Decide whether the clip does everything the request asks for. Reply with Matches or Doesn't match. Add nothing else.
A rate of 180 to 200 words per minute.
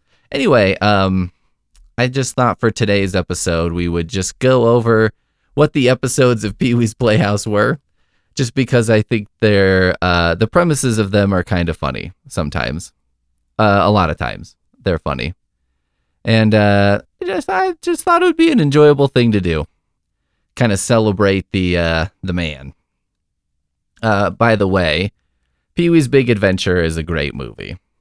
Doesn't match